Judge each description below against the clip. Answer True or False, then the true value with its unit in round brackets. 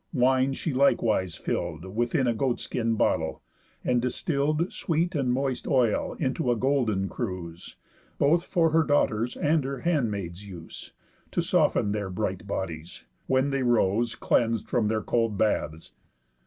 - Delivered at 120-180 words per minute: True (145 wpm)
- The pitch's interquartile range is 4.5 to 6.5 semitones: True (5.2 semitones)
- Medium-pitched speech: False (120 Hz)